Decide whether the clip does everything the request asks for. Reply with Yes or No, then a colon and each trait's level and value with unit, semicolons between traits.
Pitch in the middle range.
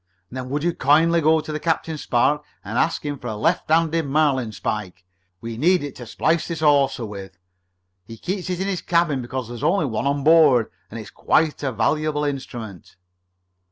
Yes: medium, 145 Hz